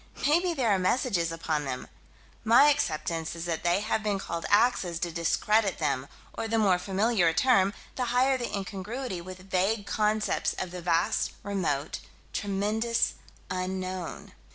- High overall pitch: Yes, high, 195 Hz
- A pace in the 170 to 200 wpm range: No, average, 155 wpm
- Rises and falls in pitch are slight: No, average, 4.5 semitones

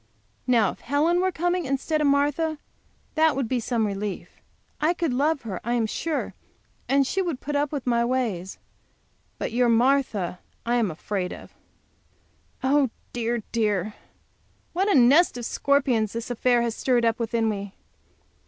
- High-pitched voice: Yes, high, 245 Hz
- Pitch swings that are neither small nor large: Yes, average, 4.4 semitones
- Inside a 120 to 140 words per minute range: No, average, 160 wpm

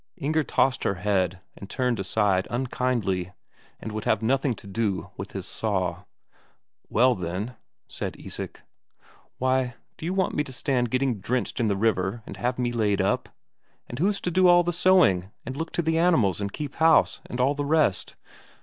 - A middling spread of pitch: No, wide, 6.3 semitones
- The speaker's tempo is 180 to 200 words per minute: Yes, average, 185 wpm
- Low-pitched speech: Yes, low, 125 Hz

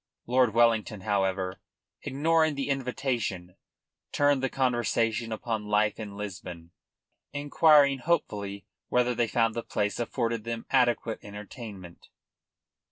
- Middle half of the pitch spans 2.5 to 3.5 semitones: No, average, 4.1 semitones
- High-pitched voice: No, low, 115 Hz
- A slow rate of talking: Yes, slow, 110 wpm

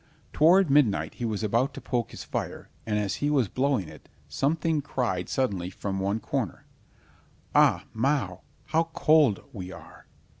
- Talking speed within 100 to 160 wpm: Yes, average, 155 wpm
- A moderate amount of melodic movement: No, wide, 6.8 semitones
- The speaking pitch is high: No, low, 120 Hz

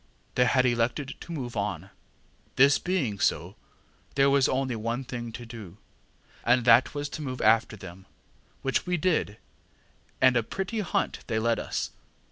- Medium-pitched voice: No, low, 125 Hz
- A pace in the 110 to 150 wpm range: No, average, 160 wpm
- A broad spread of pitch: No, average, 3.5 semitones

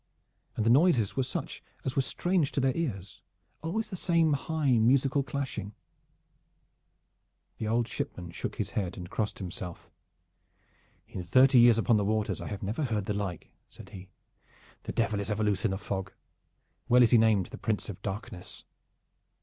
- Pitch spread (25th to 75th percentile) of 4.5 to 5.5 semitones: Yes, average, 5.1 semitones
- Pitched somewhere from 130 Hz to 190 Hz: No, low, 110 Hz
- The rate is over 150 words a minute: Yes, average, 175 wpm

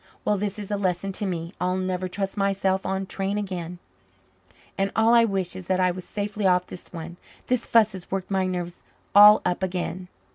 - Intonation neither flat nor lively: No, narrow, 1.9 semitones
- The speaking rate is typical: No, fast, 210 wpm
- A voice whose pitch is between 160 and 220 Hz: Yes, high, 190 Hz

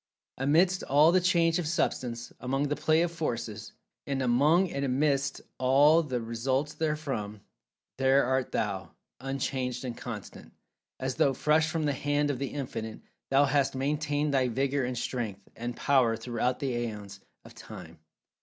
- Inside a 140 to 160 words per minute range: Yes, average, 145 wpm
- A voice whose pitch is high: No, low, 135 Hz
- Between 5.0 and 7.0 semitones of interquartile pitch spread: No, average, 3.4 semitones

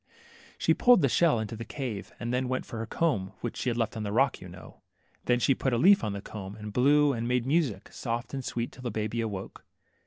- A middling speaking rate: No, fast, 250 wpm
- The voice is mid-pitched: No, low, 120 Hz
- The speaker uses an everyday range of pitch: Yes, average, 3.6 semitones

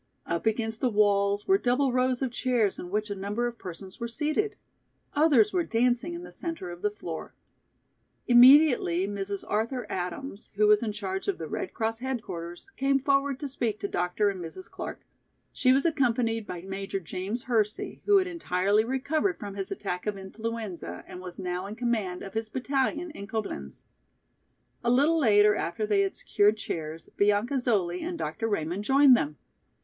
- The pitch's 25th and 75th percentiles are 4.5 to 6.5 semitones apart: Yes, average, 5.0 semitones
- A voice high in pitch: Yes, high, 220 Hz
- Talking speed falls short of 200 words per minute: Yes, average, 180 wpm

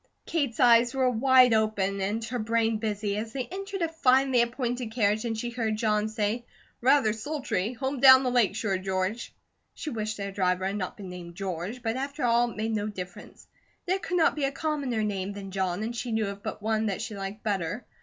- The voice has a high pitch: Yes, high, 225 Hz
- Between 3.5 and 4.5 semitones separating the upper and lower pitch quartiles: Yes, average, 3.8 semitones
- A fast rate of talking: Yes, fast, 215 wpm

